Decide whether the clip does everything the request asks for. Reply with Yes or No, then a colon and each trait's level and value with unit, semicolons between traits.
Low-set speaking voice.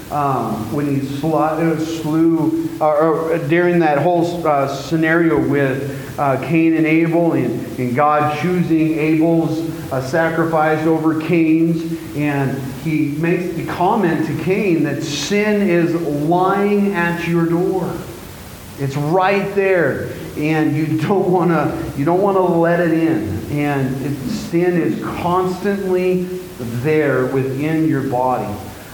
No: medium, 160 Hz